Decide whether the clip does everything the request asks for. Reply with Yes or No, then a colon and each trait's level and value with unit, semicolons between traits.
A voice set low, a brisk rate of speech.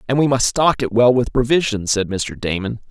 Yes: low, 120 Hz; fast, 225 wpm